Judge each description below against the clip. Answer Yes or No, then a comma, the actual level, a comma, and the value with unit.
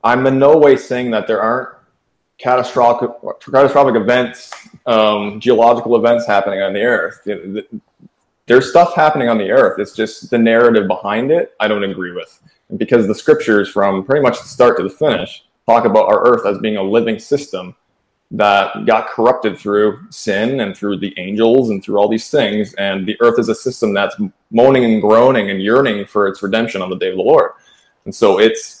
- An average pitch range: Yes, average, 4.4 semitones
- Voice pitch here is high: No, low, 115 Hz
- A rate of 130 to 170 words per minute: No, average, 190 wpm